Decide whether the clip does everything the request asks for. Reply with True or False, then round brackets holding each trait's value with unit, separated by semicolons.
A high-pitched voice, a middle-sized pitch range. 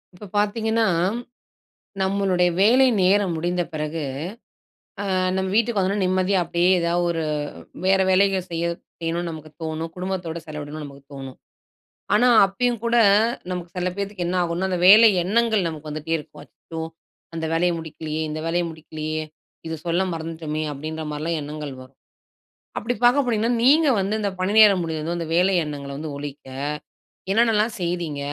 False (175 Hz; 4.0 semitones)